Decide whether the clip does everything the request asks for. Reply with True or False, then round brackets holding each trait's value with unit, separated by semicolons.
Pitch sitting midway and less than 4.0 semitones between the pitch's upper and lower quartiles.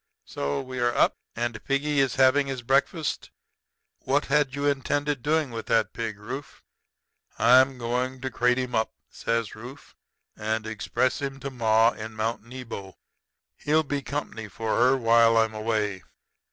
False (125 Hz; 3.4 semitones)